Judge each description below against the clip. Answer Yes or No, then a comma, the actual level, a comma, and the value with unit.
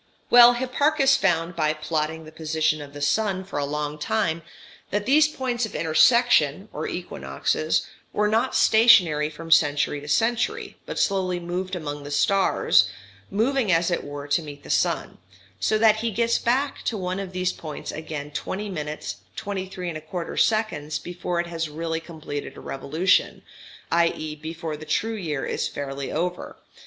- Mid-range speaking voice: Yes, medium, 170 Hz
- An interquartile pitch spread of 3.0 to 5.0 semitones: No, wide, 5.6 semitones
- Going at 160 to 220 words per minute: Yes, average, 165 wpm